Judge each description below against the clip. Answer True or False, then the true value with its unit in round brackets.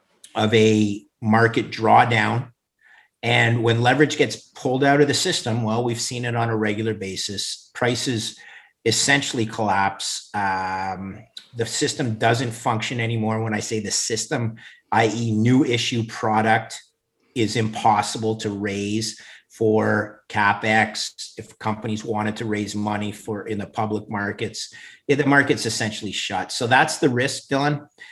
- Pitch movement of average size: False (2.2 semitones)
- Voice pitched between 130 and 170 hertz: False (110 Hz)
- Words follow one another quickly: False (140 wpm)